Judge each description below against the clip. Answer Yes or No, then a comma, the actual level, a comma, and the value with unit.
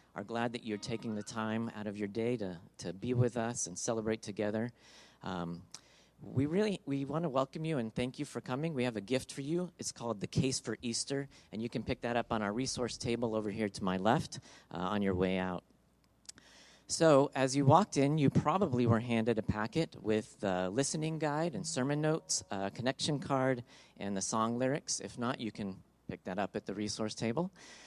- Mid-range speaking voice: No, low, 120 Hz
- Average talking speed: No, fast, 215 wpm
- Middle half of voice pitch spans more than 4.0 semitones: Yes, average, 4.5 semitones